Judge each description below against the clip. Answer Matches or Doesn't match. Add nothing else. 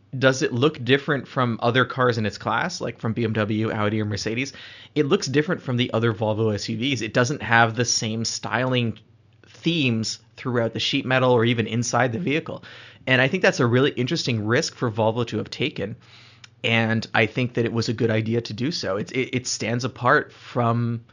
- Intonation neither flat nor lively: Doesn't match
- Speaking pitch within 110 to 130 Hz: Matches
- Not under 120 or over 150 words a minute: Doesn't match